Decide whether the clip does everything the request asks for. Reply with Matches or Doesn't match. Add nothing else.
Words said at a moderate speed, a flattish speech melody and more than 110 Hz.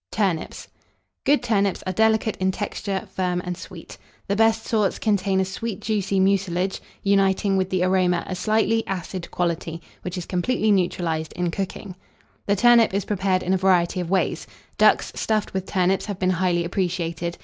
Matches